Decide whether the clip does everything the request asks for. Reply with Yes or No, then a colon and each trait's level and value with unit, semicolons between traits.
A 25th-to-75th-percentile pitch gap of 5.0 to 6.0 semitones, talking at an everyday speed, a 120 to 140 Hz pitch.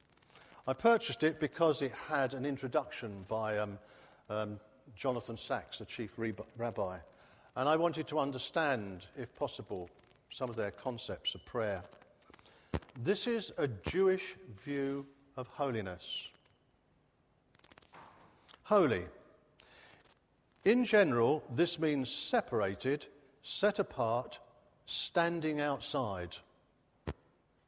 No: wide, 5.6 semitones; slow, 100 wpm; low, 135 Hz